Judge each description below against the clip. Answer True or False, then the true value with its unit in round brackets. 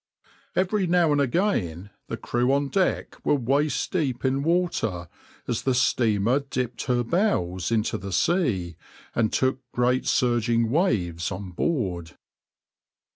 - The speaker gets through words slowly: True (130 wpm)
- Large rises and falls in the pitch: True (6.4 semitones)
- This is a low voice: True (125 Hz)